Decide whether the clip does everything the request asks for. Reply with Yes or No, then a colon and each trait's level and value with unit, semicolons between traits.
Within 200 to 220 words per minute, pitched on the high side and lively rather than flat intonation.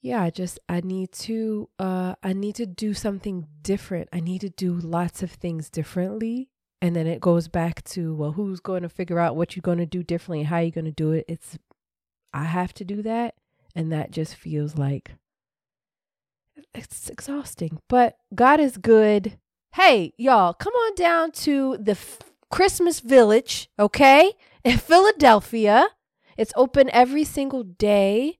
No: average, 175 wpm; high, 195 Hz; wide, 6.1 semitones